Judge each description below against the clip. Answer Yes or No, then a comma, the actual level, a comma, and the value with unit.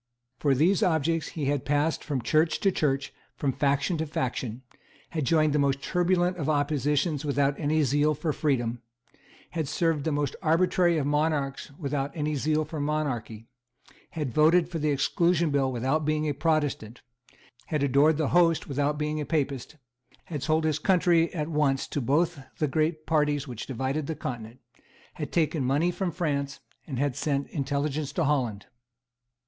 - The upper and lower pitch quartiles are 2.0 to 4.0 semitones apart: Yes, narrow, 2.4 semitones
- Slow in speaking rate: No, average, 175 wpm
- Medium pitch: Yes, medium, 150 Hz